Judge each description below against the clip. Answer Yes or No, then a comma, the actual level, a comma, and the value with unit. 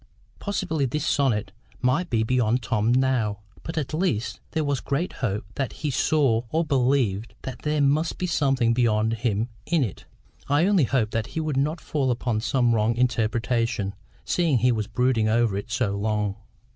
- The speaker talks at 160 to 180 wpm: Yes, average, 175 wpm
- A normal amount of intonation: Yes, average, 4.4 semitones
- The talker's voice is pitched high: No, low, 125 Hz